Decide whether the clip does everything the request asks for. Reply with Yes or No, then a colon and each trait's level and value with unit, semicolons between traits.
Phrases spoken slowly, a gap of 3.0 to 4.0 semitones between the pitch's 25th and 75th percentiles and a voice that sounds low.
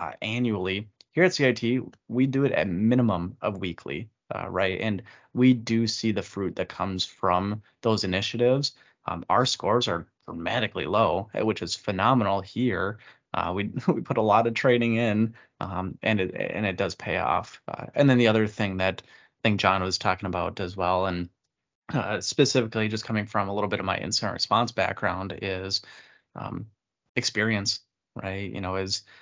No: average, 180 wpm; average, 3.6 semitones; low, 105 Hz